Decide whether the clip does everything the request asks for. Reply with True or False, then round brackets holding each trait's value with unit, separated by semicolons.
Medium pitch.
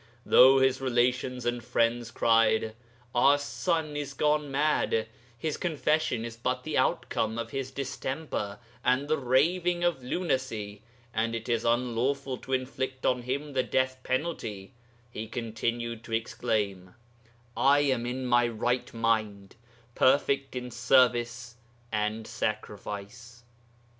False (125 Hz)